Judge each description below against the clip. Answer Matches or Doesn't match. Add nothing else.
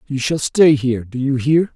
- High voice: Doesn't match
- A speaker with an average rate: Doesn't match